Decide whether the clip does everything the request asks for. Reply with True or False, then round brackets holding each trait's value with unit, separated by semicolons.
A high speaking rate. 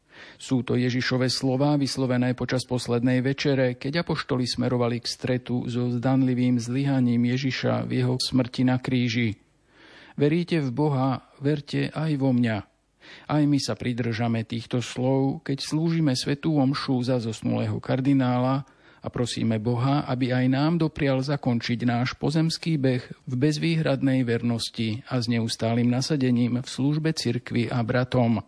False (135 wpm)